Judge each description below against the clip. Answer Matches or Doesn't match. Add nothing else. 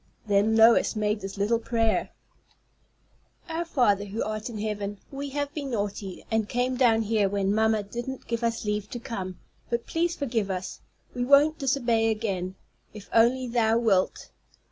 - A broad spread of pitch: Doesn't match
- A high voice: Matches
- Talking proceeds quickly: Doesn't match